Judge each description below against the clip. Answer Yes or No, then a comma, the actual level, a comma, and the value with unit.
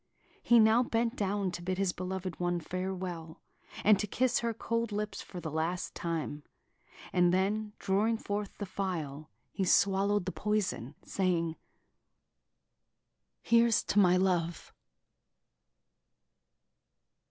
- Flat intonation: No, average, 3.1 semitones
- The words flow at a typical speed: No, slow, 120 wpm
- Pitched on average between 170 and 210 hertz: Yes, high, 190 Hz